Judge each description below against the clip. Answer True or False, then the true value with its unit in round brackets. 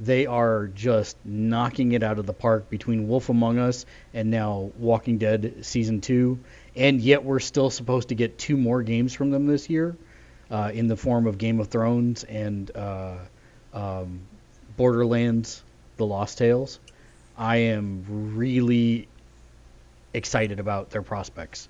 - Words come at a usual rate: True (150 wpm)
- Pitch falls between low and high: False (115 Hz)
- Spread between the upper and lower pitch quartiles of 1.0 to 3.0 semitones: True (2.6 semitones)